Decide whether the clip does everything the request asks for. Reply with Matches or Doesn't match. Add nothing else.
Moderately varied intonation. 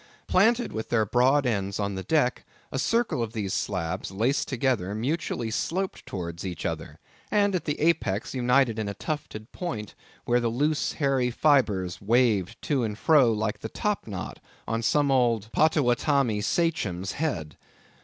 Doesn't match